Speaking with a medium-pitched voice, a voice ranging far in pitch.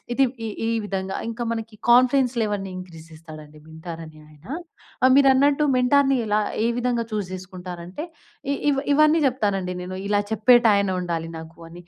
No: high, 205 Hz; wide, 6.0 semitones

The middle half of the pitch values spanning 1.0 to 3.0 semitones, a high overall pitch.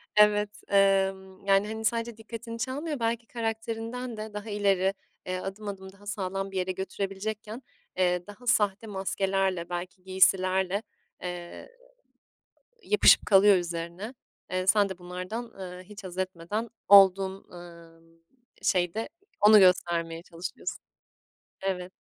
Yes: narrow, 2.6 semitones; high, 195 Hz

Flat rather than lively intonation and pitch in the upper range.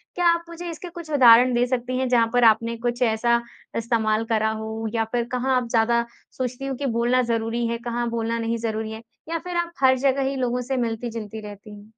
Yes: narrow, 2.3 semitones; high, 235 Hz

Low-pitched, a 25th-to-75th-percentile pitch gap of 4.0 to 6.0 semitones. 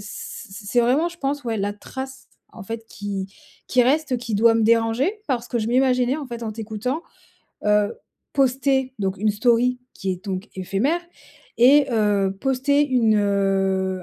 No: high, 230 Hz; average, 4.4 semitones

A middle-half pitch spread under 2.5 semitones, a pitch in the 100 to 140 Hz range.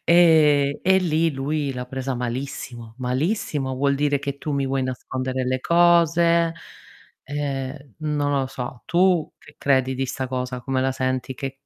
No: average, 2.8 semitones; low, 135 Hz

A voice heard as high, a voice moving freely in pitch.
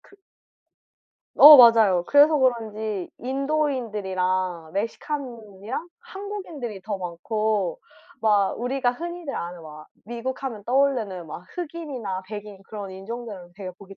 Yes: high, 220 Hz; wide, 6.0 semitones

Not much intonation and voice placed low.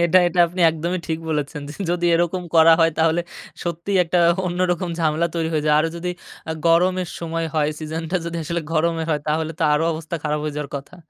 No: narrow, 1.7 semitones; medium, 165 Hz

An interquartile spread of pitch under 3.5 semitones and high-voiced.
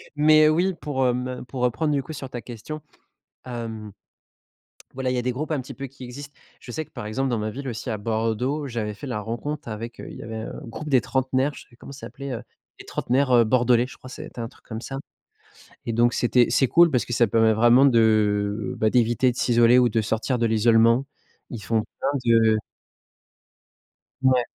No: average, 2.9 semitones; low, 120 Hz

